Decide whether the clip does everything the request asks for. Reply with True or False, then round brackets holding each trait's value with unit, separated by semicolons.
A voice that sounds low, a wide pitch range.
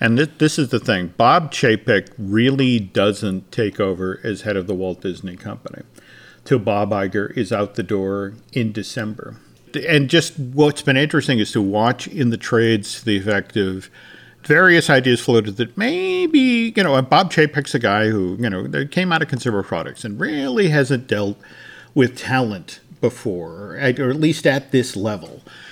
True (120 Hz; 6.2 semitones)